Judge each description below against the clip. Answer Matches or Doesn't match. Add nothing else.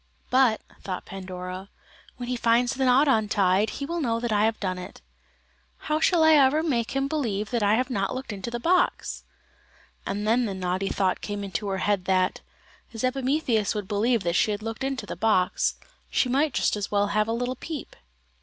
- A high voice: Matches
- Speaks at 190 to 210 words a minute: Matches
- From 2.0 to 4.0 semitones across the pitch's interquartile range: Doesn't match